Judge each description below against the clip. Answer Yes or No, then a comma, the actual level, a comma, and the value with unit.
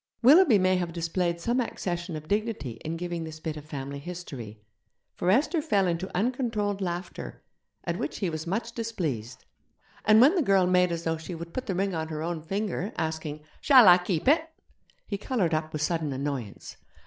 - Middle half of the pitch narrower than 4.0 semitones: No, average, 4.7 semitones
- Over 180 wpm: Yes, average, 190 wpm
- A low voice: No, medium, 175 Hz